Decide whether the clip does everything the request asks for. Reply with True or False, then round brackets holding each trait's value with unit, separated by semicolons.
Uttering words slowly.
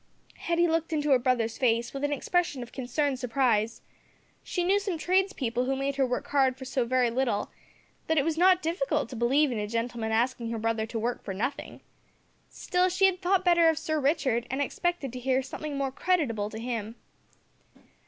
False (195 wpm)